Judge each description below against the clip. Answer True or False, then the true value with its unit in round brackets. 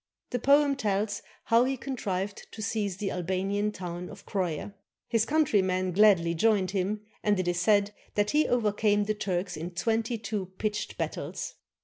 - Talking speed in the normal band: True (165 wpm)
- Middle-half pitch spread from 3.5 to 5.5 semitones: False (3.1 semitones)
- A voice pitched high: True (205 Hz)